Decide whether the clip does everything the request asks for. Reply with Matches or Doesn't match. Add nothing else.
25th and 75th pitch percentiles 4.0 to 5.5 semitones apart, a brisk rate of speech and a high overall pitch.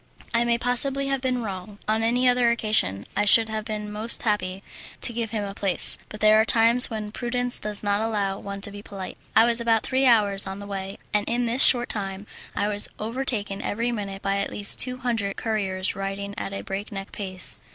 Doesn't match